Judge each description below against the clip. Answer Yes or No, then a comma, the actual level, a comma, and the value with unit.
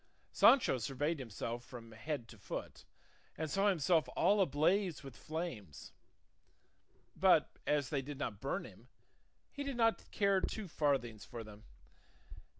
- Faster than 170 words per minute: No, average, 140 wpm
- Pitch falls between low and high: Yes, medium, 145 Hz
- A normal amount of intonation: No, wide, 7.6 semitones